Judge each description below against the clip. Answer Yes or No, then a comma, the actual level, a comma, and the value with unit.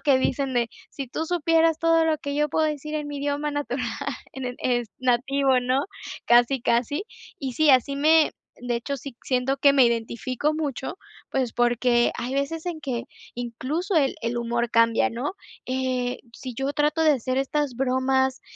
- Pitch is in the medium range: No, very high, 265 Hz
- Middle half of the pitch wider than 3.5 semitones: No, average, 3.2 semitones